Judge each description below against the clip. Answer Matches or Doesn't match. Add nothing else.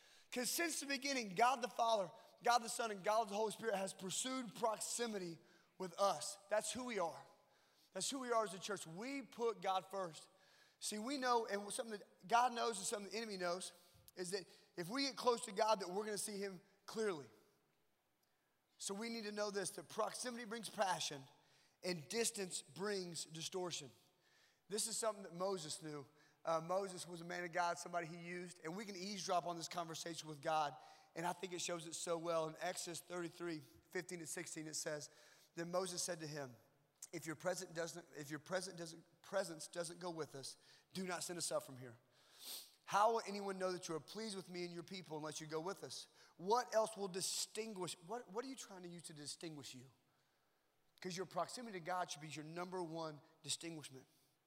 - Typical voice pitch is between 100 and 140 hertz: Doesn't match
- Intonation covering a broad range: Doesn't match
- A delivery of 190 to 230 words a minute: Matches